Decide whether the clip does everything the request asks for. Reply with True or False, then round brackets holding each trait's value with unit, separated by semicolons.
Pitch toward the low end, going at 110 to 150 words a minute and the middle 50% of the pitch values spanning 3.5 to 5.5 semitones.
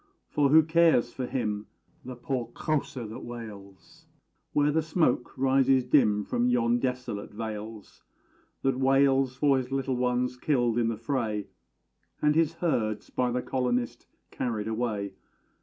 True (125 Hz; 140 wpm; 3.8 semitones)